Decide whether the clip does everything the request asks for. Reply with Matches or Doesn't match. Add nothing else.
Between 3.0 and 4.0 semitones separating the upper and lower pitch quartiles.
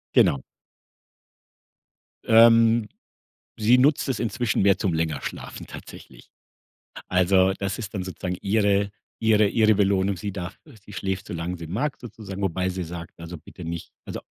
Matches